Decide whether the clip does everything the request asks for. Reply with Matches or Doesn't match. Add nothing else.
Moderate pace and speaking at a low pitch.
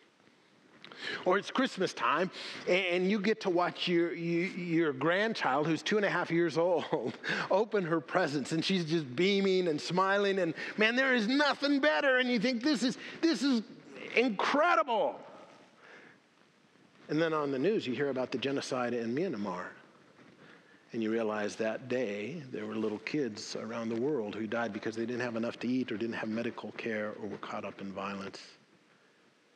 Doesn't match